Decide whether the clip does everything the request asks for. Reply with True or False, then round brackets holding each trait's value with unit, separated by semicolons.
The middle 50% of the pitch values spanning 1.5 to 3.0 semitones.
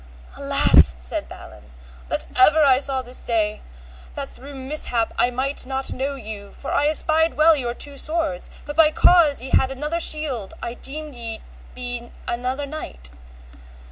False (3.8 semitones)